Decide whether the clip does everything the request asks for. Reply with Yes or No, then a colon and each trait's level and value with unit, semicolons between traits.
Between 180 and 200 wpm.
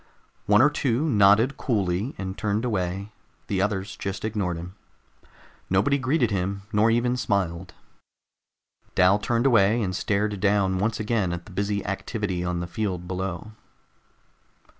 No: average, 140 wpm